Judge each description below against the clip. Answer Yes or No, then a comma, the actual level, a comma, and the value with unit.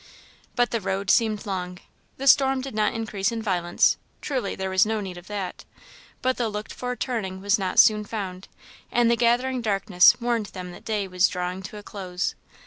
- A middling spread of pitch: Yes, average, 3.8 semitones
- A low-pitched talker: No, high, 210 Hz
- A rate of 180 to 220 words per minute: Yes, average, 190 wpm